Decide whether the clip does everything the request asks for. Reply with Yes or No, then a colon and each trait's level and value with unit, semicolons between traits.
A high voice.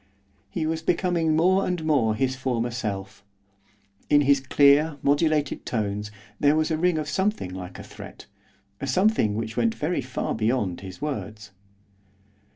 No: medium, 140 Hz